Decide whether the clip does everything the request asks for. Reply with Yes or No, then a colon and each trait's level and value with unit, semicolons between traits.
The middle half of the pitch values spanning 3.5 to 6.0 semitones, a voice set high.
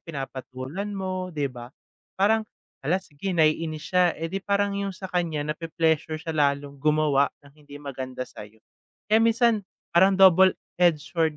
No: average, 4.7 semitones; medium, 160 Hz